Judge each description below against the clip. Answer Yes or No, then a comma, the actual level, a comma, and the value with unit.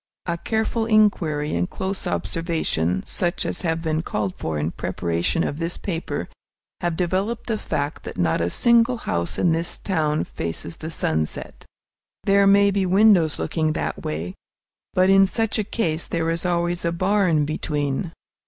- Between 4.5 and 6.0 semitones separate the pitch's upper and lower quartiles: Yes, average, 5.1 semitones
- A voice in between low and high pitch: Yes, medium, 165 Hz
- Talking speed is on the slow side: No, average, 160 wpm